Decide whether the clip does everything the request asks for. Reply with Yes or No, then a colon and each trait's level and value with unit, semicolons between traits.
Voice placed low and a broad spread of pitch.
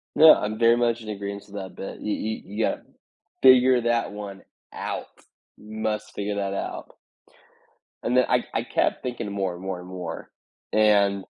No: low, 105 Hz; average, 2.8 semitones